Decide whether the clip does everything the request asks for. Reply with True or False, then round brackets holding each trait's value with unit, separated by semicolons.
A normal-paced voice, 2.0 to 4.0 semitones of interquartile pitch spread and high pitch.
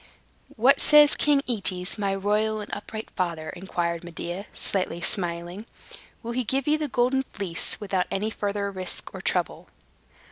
False (150 wpm; 4.6 semitones; 200 Hz)